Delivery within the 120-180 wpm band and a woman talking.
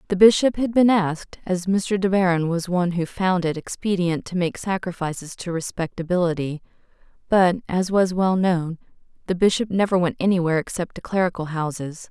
Yes: average, 170 wpm; female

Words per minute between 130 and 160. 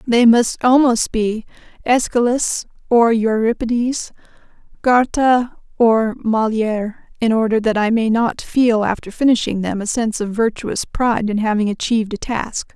Yes: average, 140 wpm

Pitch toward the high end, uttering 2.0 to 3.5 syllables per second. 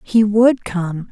Yes: high, 205 Hz; 3.0 syllables/s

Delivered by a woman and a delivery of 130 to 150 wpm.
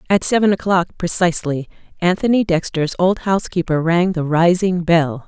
Yes: female; slow, 135 wpm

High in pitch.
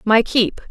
Yes: high, 220 Hz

